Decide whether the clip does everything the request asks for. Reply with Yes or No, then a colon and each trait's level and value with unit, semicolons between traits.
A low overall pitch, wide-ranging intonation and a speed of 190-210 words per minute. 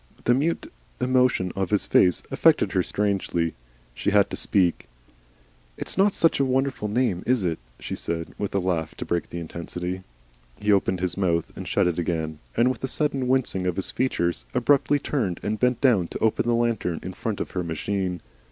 Yes: low, 100 Hz; wide, 6.3 semitones; average, 200 wpm